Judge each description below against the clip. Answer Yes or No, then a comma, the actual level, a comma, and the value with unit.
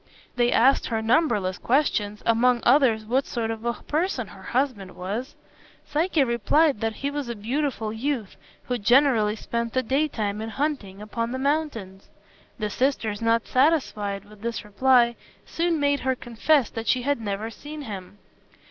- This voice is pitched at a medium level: No, high, 235 Hz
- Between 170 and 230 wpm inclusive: No, average, 160 wpm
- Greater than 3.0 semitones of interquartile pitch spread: Yes, average, 4.5 semitones